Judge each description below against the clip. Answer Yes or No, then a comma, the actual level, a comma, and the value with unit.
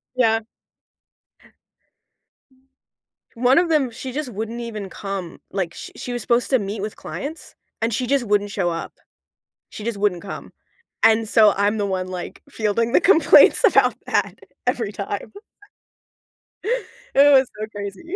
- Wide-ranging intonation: No, average, 3.9 semitones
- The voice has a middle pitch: No, high, 220 Hz